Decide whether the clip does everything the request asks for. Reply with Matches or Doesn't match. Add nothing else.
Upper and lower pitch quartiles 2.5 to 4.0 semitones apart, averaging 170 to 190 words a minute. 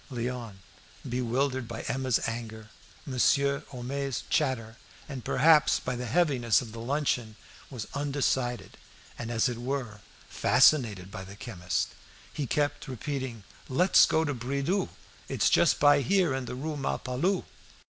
Doesn't match